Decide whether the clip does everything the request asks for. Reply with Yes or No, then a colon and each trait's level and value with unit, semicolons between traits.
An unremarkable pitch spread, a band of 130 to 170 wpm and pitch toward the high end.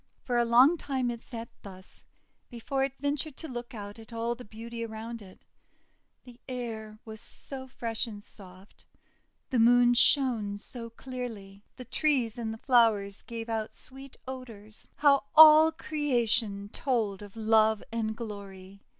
Yes: average, 3.0 semitones; average, 150 wpm; high, 230 Hz